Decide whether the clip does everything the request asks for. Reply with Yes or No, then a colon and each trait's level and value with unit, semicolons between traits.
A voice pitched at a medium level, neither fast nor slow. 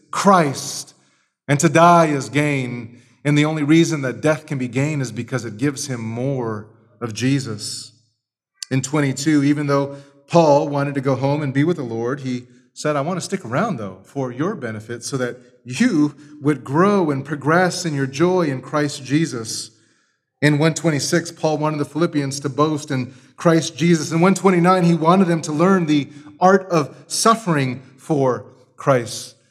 Yes: medium, 145 Hz; average, 175 wpm